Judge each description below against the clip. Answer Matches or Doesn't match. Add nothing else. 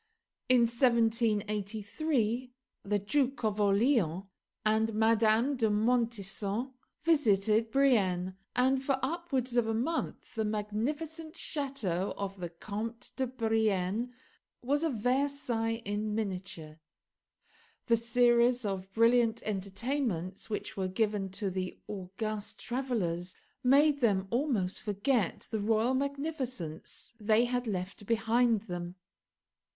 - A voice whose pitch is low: Doesn't match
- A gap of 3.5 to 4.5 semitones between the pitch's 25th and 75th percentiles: Matches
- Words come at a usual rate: Doesn't match